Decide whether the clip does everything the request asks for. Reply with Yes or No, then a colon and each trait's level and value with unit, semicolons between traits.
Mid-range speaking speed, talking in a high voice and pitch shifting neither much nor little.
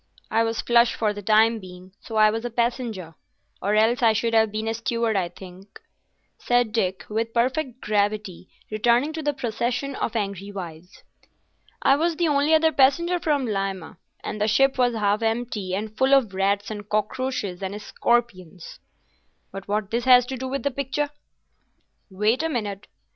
Yes: average, 175 wpm; high, 225 Hz; average, 3.9 semitones